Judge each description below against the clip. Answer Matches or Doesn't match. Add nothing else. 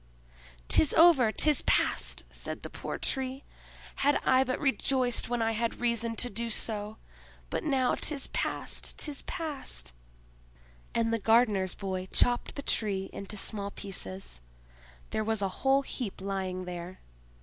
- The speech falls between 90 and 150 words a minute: Matches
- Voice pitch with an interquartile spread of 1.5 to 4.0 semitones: Doesn't match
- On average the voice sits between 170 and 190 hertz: Doesn't match